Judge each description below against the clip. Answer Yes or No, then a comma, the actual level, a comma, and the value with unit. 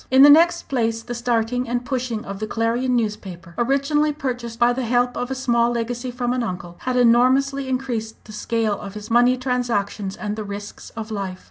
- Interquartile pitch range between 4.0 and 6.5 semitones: No, average, 2.7 semitones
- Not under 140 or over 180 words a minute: No, average, 200 wpm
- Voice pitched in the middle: No, high, 240 Hz